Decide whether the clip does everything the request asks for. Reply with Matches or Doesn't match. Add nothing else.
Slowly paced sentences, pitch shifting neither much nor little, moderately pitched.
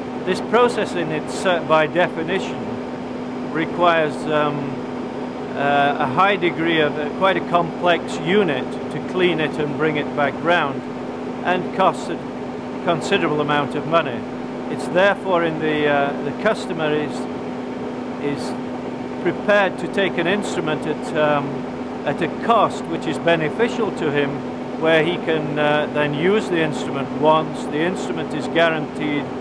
Doesn't match